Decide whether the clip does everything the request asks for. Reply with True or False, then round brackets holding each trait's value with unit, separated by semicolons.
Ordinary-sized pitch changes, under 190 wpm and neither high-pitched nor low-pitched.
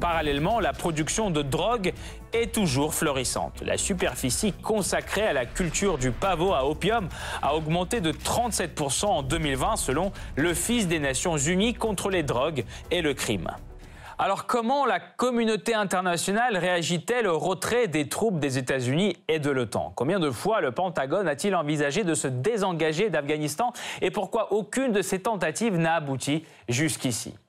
False (6.4 semitones; 155 wpm; 175 Hz)